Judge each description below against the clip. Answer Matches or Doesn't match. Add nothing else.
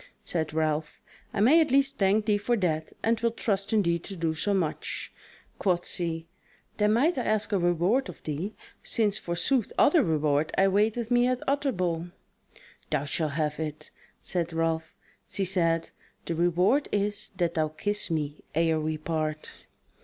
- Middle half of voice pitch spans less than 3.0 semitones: Doesn't match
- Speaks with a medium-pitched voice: Matches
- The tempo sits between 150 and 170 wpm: Matches